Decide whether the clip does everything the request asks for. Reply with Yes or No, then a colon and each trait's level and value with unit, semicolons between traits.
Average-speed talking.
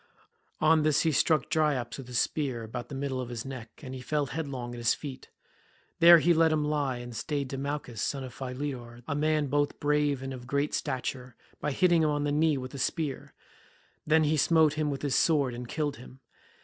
No: fast, 215 wpm